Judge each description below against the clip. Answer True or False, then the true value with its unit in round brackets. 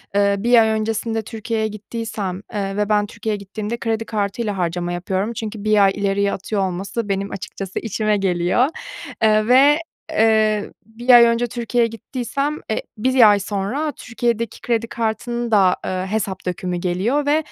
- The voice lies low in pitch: False (215 Hz)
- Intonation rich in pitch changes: False (2.8 semitones)